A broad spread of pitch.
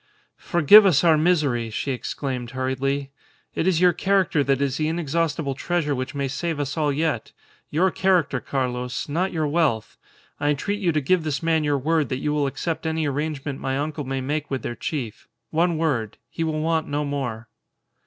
No: average, 3.3 semitones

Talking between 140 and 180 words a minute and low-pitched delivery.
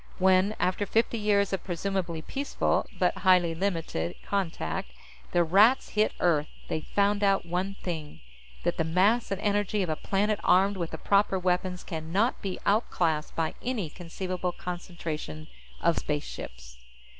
No: average, 155 wpm; medium, 185 Hz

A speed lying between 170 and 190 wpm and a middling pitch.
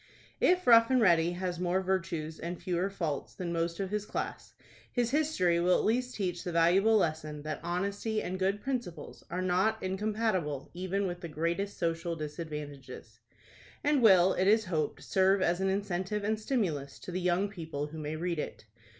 Yes: average, 180 wpm; medium, 180 Hz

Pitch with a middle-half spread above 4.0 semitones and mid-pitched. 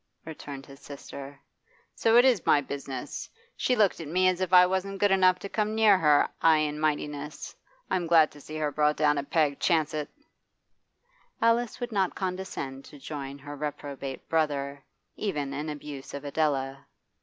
Yes: average, 4.6 semitones; medium, 150 Hz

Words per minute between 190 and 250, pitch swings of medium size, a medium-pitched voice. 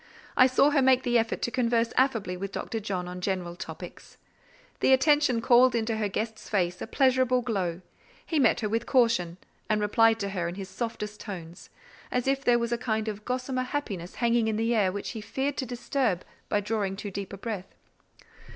No: average, 200 wpm; average, 4.1 semitones; high, 225 Hz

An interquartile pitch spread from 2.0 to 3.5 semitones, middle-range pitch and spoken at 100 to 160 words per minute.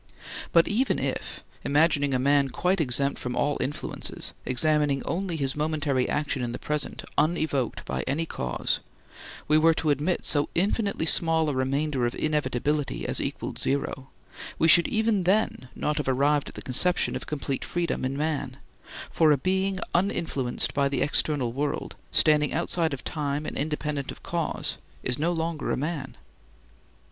Yes: average, 3.0 semitones; medium, 150 Hz; average, 155 wpm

